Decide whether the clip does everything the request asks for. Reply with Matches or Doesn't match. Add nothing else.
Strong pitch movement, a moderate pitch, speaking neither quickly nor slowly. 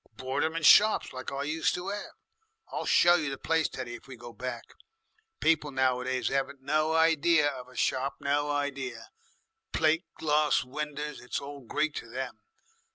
Doesn't match